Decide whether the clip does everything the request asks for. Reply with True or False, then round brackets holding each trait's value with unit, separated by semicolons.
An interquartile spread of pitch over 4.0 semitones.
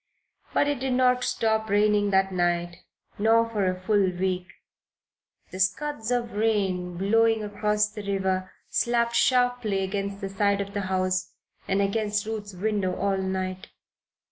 False (2.7 semitones)